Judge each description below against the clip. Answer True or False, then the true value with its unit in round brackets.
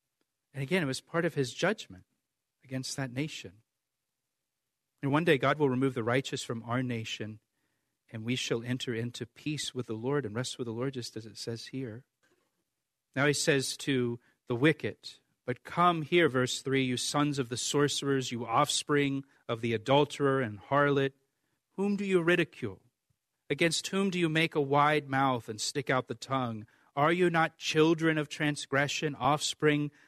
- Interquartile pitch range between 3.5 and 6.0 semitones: False (3.1 semitones)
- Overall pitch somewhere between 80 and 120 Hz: False (135 Hz)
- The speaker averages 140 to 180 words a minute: True (175 wpm)